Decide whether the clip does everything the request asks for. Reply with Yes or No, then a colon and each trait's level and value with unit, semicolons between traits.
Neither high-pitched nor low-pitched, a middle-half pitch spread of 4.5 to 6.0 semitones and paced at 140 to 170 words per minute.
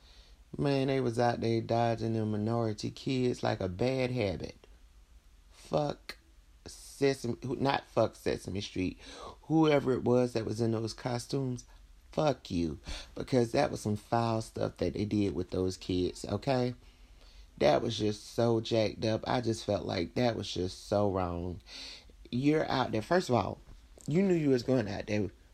No: low, 110 Hz; wide, 5.6 semitones; average, 165 wpm